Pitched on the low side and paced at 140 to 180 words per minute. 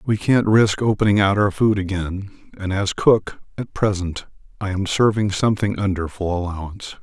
Yes: low, 100 Hz; average, 170 wpm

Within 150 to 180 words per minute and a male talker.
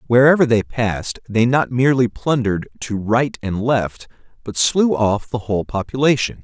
Yes: average, 160 wpm; male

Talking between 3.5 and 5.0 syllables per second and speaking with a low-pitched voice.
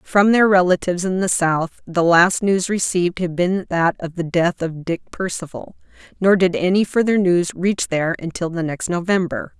No: 4.9 syllables/s; medium, 180 Hz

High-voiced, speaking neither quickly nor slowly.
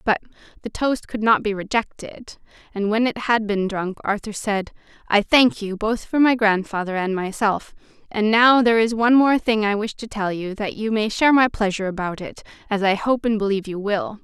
No: high, 215 Hz; fast, 215 wpm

